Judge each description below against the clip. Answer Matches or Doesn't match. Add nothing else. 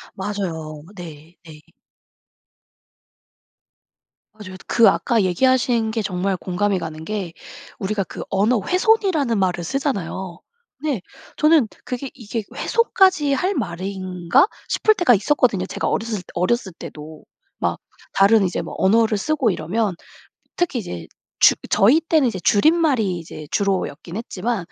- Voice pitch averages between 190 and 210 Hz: Matches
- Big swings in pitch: Matches